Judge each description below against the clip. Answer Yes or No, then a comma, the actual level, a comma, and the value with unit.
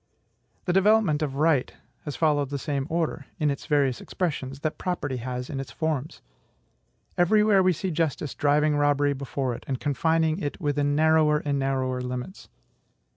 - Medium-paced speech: Yes, average, 165 wpm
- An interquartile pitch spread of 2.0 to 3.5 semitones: Yes, average, 2.9 semitones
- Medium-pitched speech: Yes, medium, 145 Hz